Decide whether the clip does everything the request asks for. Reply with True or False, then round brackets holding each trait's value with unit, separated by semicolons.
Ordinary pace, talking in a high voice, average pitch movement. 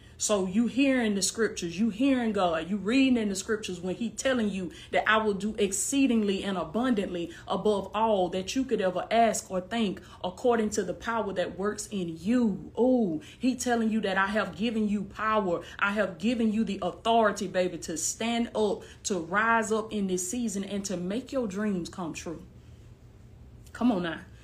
True (190 wpm; 210 Hz; 3.4 semitones)